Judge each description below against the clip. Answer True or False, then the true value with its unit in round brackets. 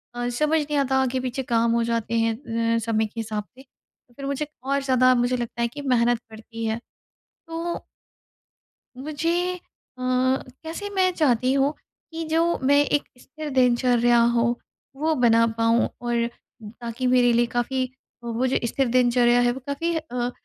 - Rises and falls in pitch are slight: False (3.2 semitones)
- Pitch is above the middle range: True (250 Hz)